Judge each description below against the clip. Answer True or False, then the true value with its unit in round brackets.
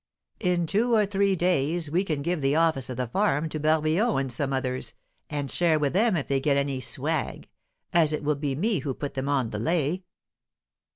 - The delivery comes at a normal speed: False (210 wpm)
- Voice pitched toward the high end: False (150 Hz)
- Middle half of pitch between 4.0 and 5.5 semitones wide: True (4.4 semitones)